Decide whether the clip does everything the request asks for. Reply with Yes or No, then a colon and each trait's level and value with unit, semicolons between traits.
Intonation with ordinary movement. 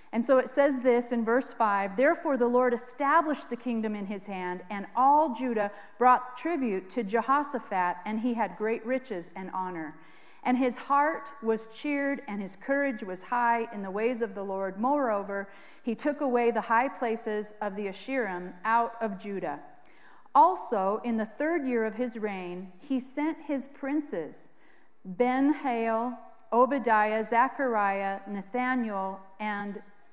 Yes: average, 4.1 semitones